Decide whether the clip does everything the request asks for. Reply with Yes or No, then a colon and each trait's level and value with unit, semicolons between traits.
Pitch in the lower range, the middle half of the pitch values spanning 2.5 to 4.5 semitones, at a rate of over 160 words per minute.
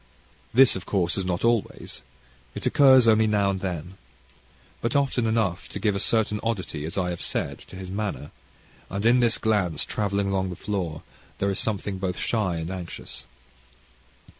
Yes: low, 100 Hz; average, 3.3 semitones; average, 170 wpm